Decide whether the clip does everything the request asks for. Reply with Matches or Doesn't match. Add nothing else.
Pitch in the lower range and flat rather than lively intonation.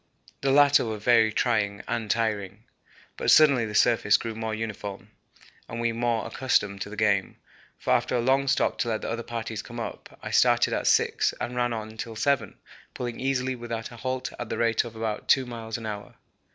Matches